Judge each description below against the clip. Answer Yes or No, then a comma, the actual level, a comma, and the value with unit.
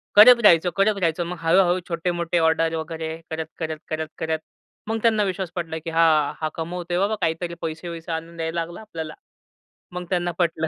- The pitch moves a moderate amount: No, narrow, 1.8 semitones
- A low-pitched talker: No, medium, 170 Hz